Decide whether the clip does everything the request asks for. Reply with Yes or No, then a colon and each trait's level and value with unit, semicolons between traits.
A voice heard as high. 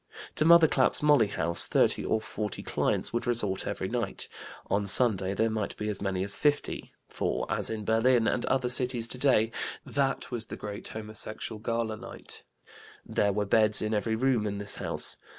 No: low, 110 Hz